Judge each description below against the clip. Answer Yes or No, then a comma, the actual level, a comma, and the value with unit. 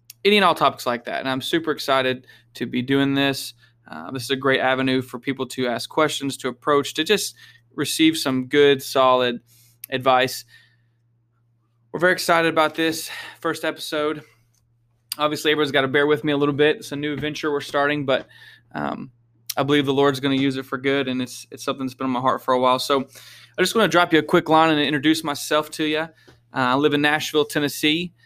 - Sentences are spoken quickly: Yes, fast, 215 wpm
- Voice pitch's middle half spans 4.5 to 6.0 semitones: No, average, 3.2 semitones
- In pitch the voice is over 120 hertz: Yes, medium, 140 Hz